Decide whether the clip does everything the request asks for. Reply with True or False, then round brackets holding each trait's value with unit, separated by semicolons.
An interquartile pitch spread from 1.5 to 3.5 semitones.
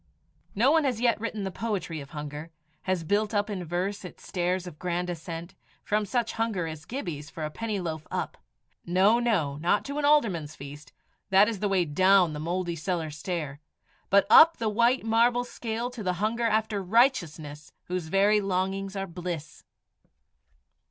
False (4.9 semitones)